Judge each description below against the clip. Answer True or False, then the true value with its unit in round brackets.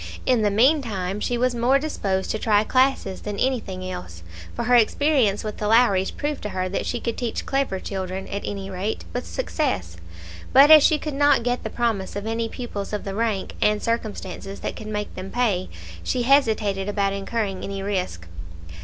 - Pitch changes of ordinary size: True (4.0 semitones)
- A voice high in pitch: True (215 Hz)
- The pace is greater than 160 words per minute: True (190 wpm)